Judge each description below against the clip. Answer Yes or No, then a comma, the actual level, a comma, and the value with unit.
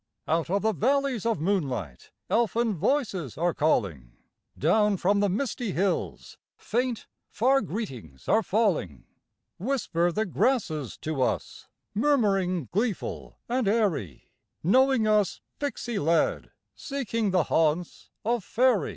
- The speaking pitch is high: Yes, high, 200 Hz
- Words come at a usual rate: No, slow, 120 wpm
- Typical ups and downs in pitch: No, wide, 6.3 semitones